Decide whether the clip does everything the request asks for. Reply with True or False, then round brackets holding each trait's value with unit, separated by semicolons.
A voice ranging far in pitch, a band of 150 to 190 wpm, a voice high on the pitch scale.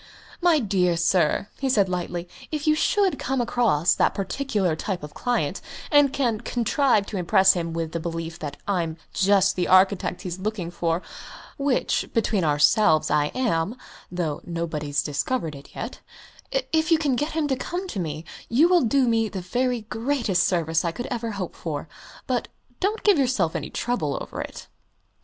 True (7.2 semitones; 175 wpm; 195 Hz)